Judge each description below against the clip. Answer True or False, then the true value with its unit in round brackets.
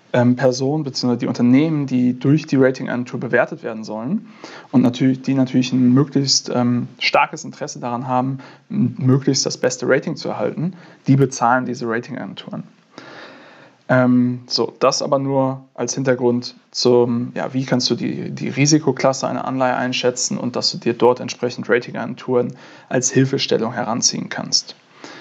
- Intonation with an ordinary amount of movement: False (1.9 semitones)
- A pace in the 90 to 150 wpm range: True (145 wpm)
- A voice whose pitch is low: True (130 Hz)